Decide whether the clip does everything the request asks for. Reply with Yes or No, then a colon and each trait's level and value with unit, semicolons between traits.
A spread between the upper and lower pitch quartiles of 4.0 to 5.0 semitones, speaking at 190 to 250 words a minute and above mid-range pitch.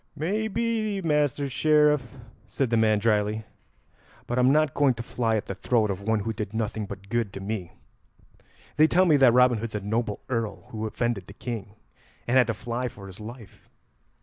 No: average, 4.6 semitones; average, 195 wpm; low, 115 Hz